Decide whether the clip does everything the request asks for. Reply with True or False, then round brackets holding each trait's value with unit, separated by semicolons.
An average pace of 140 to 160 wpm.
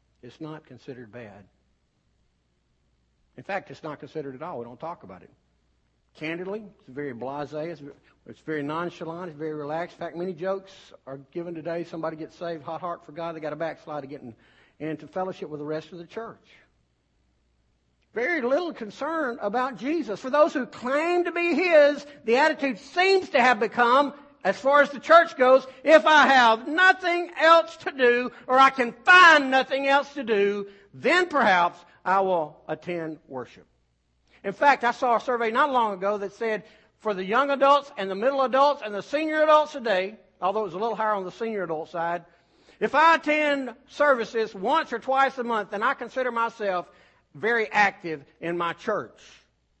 False (185 wpm)